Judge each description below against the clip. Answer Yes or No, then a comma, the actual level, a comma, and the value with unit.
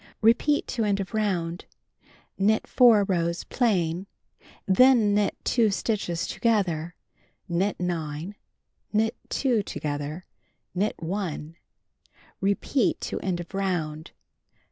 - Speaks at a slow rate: Yes, slow, 105 wpm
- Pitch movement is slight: No, average, 4.2 semitones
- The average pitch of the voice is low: No, high, 195 Hz